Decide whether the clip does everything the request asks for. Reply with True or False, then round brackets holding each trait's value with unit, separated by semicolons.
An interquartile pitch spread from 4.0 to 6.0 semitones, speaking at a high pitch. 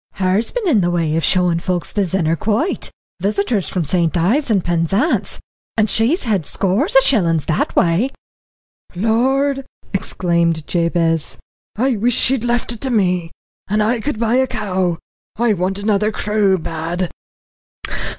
True (5.0 semitones; 200 Hz)